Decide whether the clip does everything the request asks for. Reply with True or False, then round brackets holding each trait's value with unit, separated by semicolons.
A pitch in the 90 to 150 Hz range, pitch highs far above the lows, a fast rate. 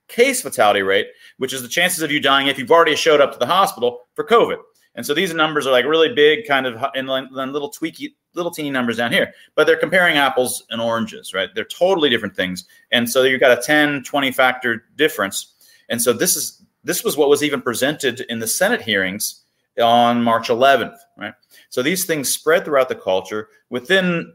True (140 Hz; 6.1 semitones; 210 wpm)